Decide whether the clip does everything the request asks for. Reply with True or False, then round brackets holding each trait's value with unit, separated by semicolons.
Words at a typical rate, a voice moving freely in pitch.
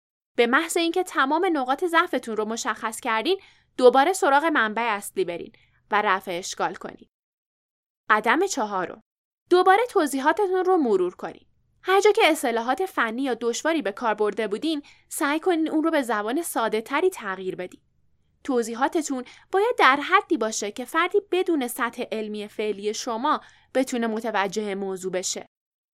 True (145 wpm; 7.4 semitones)